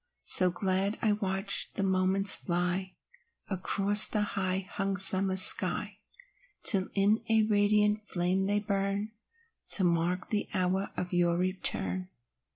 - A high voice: Yes, high, 195 Hz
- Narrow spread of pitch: Yes, narrow, 1.8 semitones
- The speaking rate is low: Yes, slow, 130 wpm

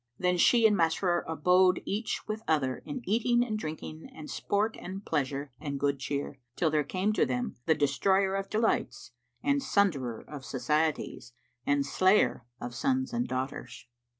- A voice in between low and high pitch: Yes, medium, 175 Hz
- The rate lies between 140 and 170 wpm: Yes, average, 160 wpm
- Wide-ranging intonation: Yes, wide, 6.9 semitones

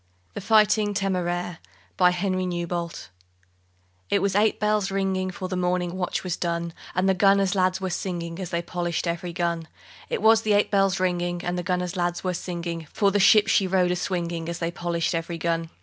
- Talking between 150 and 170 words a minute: No, average, 180 wpm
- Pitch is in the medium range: Yes, medium, 180 Hz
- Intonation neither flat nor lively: No, narrow, 2.0 semitones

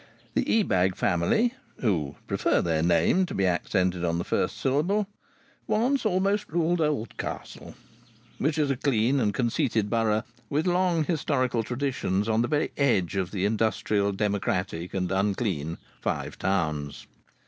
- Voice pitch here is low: Yes, low, 110 Hz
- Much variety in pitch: Yes, wide, 8.3 semitones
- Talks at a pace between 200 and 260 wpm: No, average, 140 wpm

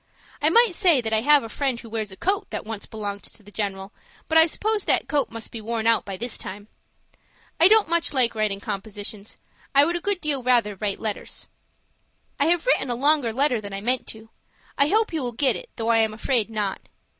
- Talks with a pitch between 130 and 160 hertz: No, high, 235 Hz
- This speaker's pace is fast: Yes, fast, 225 wpm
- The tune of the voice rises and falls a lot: Yes, wide, 5.9 semitones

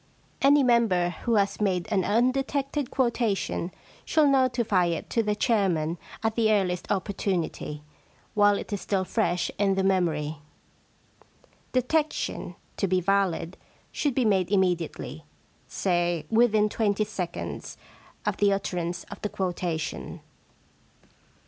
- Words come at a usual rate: No, slow, 130 wpm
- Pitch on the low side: No, high, 200 Hz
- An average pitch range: Yes, average, 4.4 semitones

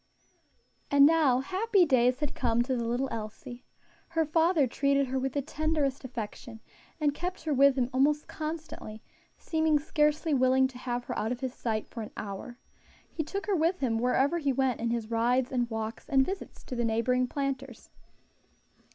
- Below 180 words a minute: No, average, 185 wpm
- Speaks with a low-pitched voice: No, very high, 265 Hz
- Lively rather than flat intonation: No, average, 3.9 semitones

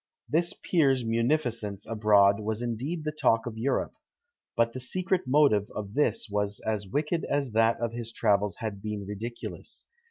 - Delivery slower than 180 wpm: Yes, average, 160 wpm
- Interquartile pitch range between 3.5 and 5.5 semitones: Yes, average, 4.8 semitones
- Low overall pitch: Yes, low, 115 Hz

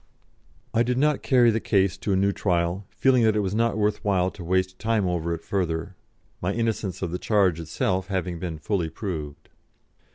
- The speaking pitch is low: Yes, very low, 95 Hz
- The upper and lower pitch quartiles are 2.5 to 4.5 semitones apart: Yes, average, 3.6 semitones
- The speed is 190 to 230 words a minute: Yes, average, 195 wpm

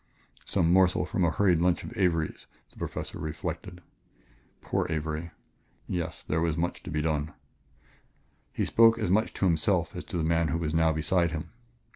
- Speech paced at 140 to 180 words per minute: Yes, average, 175 wpm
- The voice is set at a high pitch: No, very low, 85 Hz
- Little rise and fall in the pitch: Yes, narrow, 2.3 semitones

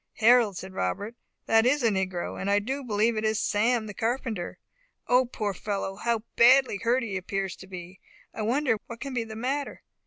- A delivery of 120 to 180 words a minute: No, average, 195 wpm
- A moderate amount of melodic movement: Yes, average, 3.6 semitones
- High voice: Yes, high, 220 Hz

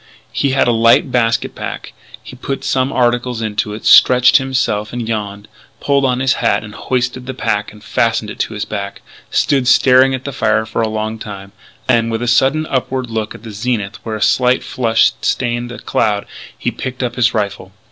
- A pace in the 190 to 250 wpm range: Yes, average, 200 wpm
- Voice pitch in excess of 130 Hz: No, low, 120 Hz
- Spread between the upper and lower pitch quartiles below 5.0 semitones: Yes, average, 2.9 semitones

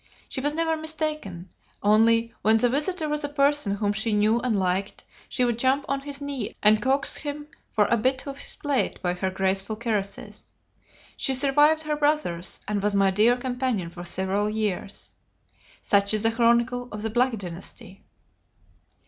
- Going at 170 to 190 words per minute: Yes, average, 175 wpm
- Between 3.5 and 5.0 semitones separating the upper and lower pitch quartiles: No, wide, 5.5 semitones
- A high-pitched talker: Yes, high, 230 Hz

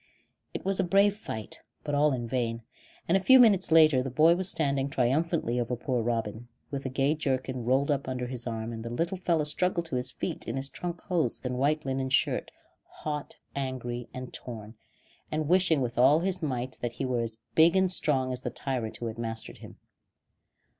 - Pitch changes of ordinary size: Yes, average, 4.7 semitones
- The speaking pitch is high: No, low, 135 Hz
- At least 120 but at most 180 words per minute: No, fast, 205 wpm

